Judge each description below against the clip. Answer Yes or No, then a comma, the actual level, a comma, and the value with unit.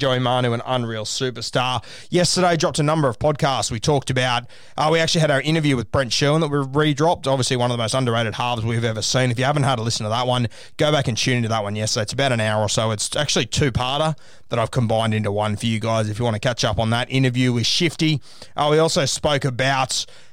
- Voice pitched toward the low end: Yes, low, 130 Hz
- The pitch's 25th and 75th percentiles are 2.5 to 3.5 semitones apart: No, average, 4.2 semitones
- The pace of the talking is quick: Yes, fast, 255 wpm